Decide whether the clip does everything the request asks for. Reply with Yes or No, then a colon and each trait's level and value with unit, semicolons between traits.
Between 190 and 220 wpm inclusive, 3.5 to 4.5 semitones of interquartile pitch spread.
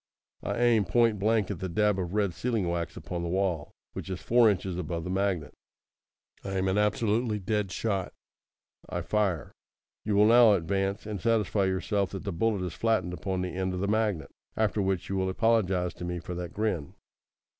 No: average, 195 wpm; average, 2.9 semitones